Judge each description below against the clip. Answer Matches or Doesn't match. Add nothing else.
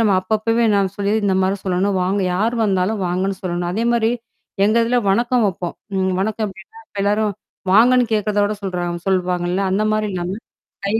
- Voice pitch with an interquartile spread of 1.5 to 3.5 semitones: Matches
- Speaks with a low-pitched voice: Doesn't match